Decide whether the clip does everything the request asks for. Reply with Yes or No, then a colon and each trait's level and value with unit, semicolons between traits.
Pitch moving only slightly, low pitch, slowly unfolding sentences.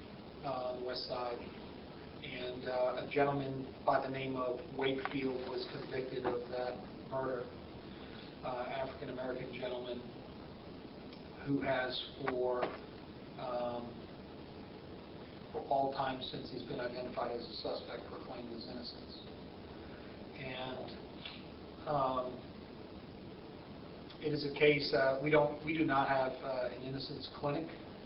Yes: narrow, 1.7 semitones; low, 130 Hz; slow, 120 wpm